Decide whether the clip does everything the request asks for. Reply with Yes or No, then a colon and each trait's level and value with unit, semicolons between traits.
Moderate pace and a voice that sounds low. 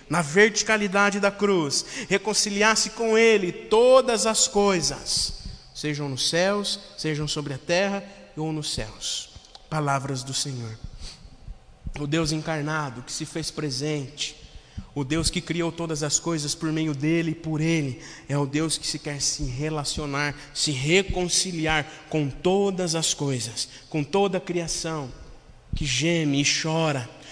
No: average, 145 wpm; medium, 155 Hz